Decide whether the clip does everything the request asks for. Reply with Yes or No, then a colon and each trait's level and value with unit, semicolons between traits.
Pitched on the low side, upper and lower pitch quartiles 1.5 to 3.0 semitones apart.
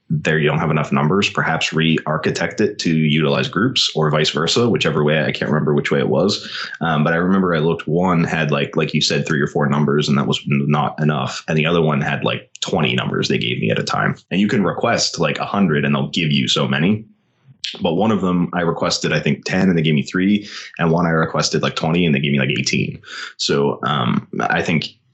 Yes: very low, 80 Hz; narrow, 2.5 semitones